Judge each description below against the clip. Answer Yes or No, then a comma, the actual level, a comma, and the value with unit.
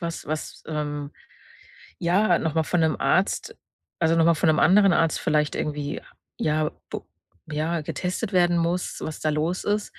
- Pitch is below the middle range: No, medium, 160 Hz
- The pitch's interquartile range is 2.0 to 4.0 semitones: Yes, narrow, 2.4 semitones